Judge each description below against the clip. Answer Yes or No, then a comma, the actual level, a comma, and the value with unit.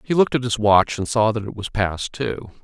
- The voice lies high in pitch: No, low, 115 Hz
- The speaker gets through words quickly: Yes, fast, 275 wpm